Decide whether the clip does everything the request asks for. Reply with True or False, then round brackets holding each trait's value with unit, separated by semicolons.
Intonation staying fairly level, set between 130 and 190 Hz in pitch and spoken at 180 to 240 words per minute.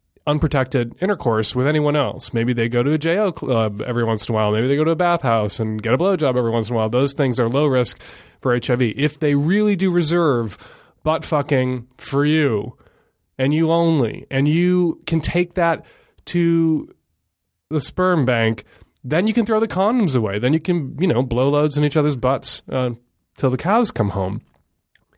False (5.6 semitones; 140 Hz; 205 wpm)